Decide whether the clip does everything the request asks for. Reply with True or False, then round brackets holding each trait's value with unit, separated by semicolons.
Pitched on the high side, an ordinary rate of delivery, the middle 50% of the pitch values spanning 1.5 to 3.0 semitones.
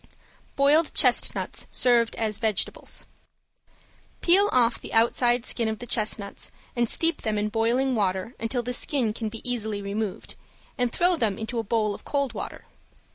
True (230 Hz; 160 wpm; 2.5 semitones)